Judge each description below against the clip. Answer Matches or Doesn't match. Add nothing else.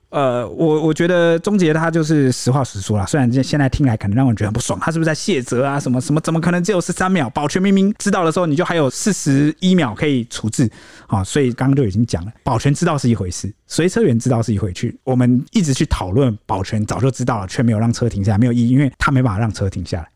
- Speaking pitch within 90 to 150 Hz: Matches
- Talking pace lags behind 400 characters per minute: Doesn't match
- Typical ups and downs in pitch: Doesn't match